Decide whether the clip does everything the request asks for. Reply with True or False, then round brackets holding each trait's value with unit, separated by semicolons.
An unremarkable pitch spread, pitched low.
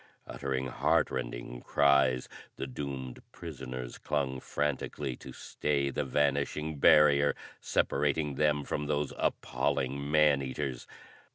False (2.0 semitones; 70 Hz)